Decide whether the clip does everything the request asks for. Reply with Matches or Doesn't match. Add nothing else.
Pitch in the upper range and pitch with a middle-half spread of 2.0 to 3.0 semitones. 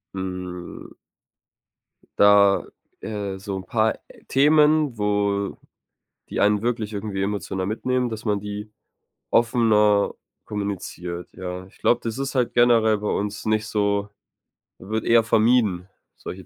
Doesn't match